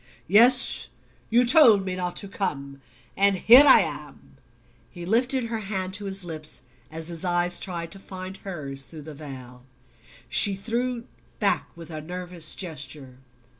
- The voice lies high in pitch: No, medium, 180 Hz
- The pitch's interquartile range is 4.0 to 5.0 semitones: Yes, average, 4.7 semitones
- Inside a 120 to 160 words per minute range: Yes, average, 155 wpm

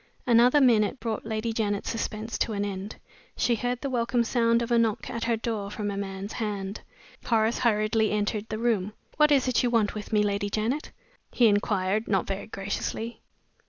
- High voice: Yes, high, 220 Hz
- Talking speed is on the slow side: No, average, 190 wpm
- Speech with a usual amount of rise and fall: No, narrow, 2.3 semitones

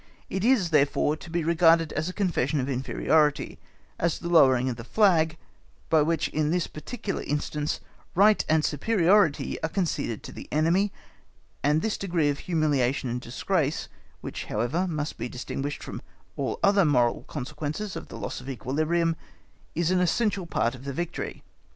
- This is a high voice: No, medium, 155 Hz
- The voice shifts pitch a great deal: No, average, 3.7 semitones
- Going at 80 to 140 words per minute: No, average, 165 wpm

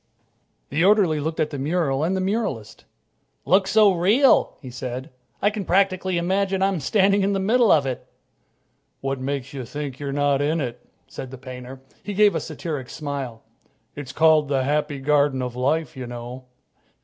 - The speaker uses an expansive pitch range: Yes, wide, 6.2 semitones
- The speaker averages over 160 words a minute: Yes, average, 180 wpm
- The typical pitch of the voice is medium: Yes, medium, 150 Hz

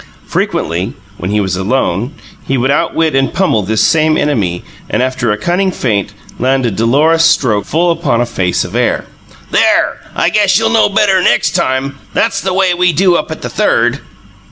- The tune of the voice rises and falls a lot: Yes, wide, 7.6 semitones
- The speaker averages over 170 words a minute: Yes, average, 185 wpm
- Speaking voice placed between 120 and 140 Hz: Yes, low, 135 Hz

